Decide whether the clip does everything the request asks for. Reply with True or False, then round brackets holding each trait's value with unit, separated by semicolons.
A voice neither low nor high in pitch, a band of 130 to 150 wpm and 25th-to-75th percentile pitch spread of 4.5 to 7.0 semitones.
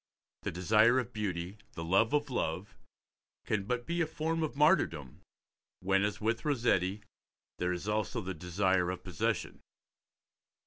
False (105 Hz; 145 wpm; 5.2 semitones)